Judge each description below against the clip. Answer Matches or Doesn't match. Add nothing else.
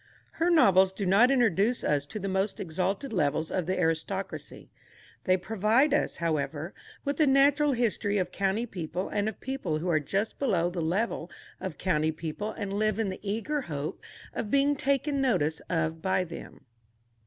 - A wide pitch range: Matches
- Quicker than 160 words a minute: Matches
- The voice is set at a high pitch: Matches